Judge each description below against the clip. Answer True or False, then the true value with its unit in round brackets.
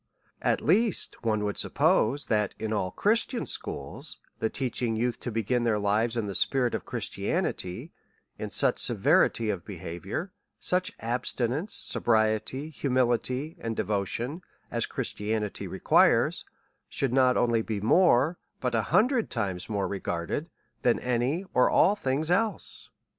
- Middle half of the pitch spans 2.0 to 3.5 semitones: False (4.8 semitones)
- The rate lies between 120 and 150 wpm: True (135 wpm)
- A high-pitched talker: False (120 Hz)